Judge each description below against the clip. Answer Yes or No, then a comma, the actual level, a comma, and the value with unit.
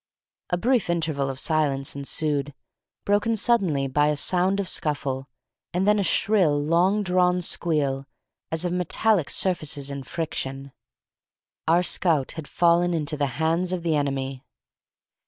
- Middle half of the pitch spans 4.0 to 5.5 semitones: Yes, average, 4.3 semitones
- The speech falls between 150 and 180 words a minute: No, average, 140 wpm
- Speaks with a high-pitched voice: No, medium, 160 Hz